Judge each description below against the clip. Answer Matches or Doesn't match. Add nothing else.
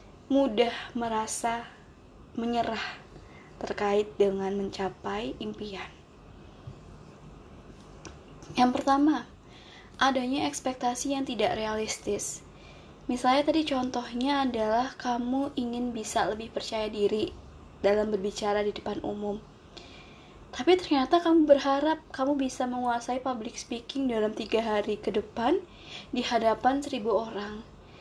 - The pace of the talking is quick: Doesn't match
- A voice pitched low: Doesn't match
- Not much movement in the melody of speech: Doesn't match